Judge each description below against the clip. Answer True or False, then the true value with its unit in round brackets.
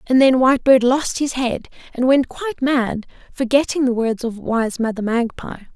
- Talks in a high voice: True (250 Hz)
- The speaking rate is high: False (175 wpm)